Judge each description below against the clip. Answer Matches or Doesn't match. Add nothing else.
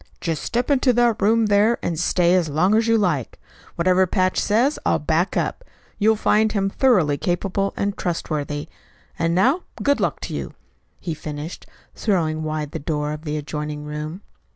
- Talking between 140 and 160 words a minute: Doesn't match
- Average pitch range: Doesn't match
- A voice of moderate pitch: Matches